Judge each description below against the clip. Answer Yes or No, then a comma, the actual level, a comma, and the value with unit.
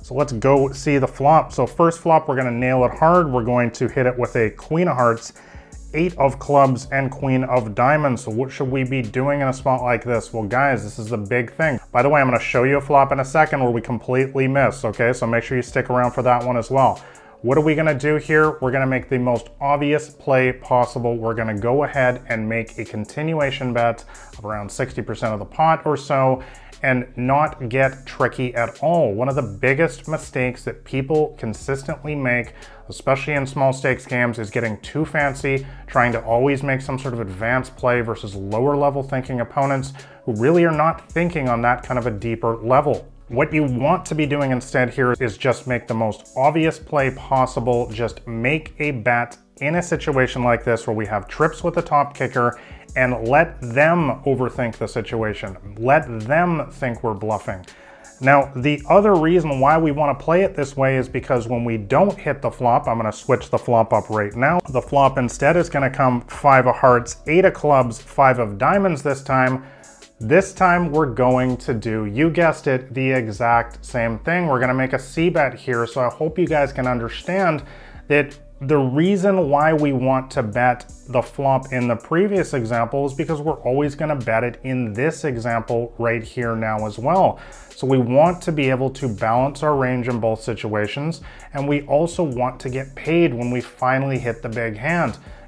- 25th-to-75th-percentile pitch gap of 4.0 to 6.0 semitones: No, average, 3.3 semitones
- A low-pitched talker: Yes, low, 130 Hz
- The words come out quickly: Yes, fast, 210 wpm